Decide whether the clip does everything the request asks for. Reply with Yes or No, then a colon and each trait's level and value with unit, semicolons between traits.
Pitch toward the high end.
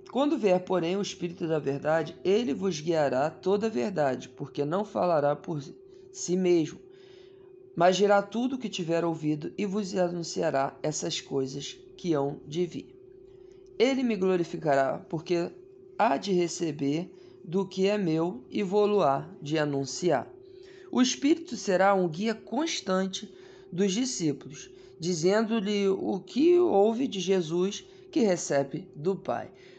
Yes: high, 195 Hz